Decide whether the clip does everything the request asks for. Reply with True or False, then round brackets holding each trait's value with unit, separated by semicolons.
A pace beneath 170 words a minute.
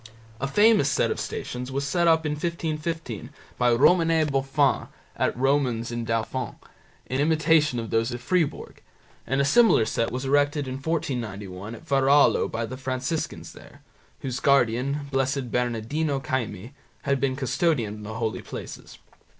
True (150 wpm)